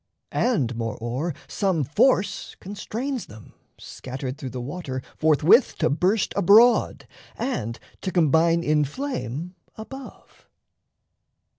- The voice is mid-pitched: Yes, medium, 165 Hz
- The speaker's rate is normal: No, slow, 105 wpm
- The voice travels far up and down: Yes, wide, 8.3 semitones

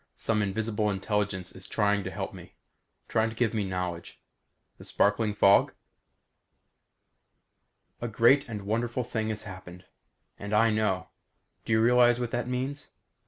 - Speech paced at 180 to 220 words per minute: No, average, 145 wpm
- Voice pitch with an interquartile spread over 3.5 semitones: No, average, 2.8 semitones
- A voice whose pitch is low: Yes, low, 110 Hz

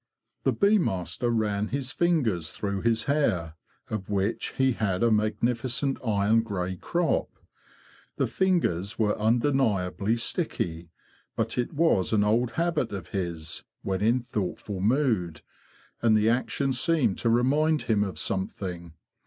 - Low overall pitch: Yes, low, 110 Hz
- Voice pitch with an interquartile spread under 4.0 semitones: No, average, 5.0 semitones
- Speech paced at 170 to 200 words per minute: No, slow, 135 wpm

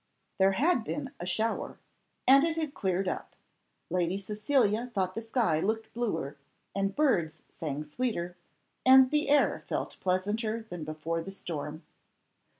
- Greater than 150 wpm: No, average, 145 wpm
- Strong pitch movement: Yes, wide, 6.1 semitones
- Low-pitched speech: No, high, 200 Hz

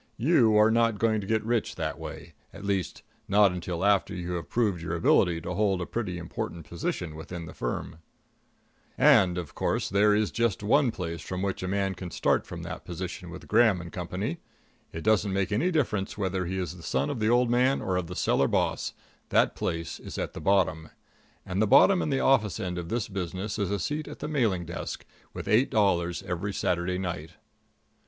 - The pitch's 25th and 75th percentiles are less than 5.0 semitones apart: Yes, average, 3.8 semitones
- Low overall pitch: Yes, very low, 95 Hz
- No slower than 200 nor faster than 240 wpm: Yes, fast, 205 wpm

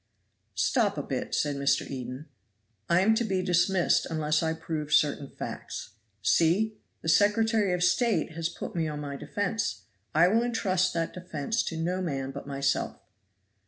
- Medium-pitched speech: Yes, medium, 165 Hz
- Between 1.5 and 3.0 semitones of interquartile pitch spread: No, average, 4.5 semitones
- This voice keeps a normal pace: Yes, average, 160 wpm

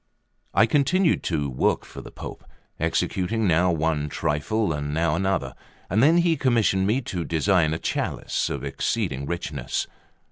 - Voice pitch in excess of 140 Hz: No, very low, 90 Hz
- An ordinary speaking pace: Yes, average, 150 wpm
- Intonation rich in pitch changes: Yes, wide, 6.3 semitones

